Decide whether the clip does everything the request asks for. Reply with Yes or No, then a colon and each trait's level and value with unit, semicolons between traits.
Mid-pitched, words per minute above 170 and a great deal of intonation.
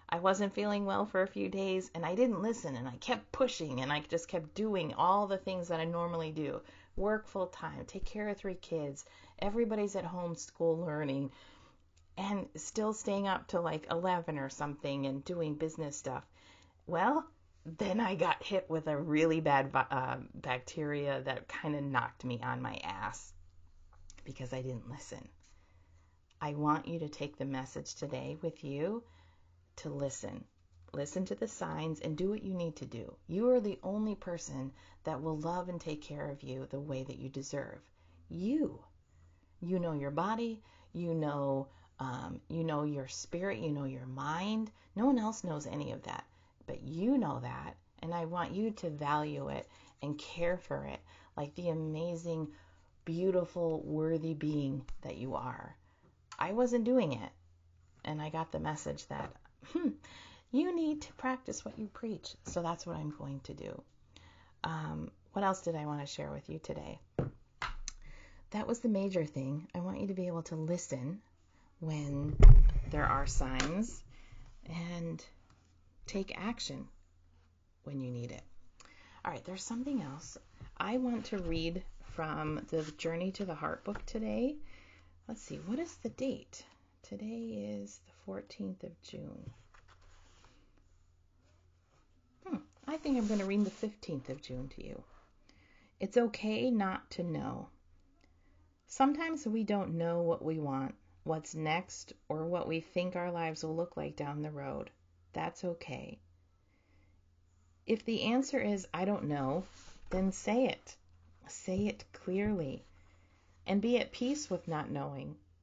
No: medium, 155 Hz; average, 165 wpm; wide, 8.5 semitones